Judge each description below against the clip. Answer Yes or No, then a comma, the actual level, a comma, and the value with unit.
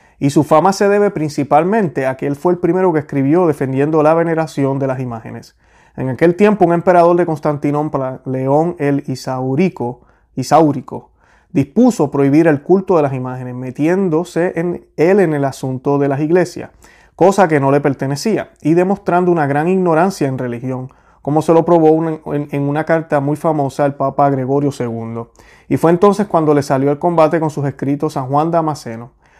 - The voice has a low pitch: No, medium, 150 Hz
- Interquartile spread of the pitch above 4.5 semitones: No, average, 3.7 semitones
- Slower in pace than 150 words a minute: No, average, 180 wpm